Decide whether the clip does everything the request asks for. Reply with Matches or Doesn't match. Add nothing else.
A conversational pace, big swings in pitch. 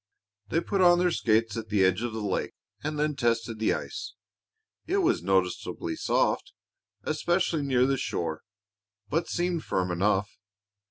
Matches